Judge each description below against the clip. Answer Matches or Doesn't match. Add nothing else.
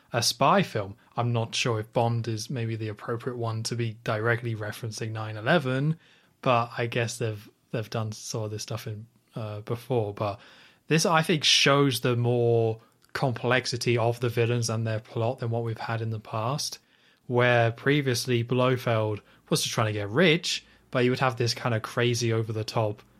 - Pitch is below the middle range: Matches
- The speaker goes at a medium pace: Matches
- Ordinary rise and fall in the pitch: Doesn't match